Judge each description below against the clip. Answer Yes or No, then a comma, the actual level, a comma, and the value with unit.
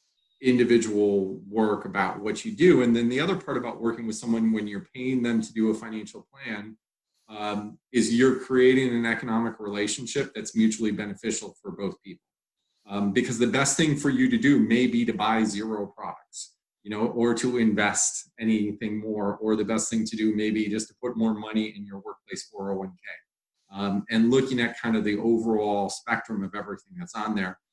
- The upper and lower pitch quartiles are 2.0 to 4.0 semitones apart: Yes, narrow, 2.4 semitones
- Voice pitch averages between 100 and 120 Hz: Yes, low, 110 Hz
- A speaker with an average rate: Yes, average, 195 wpm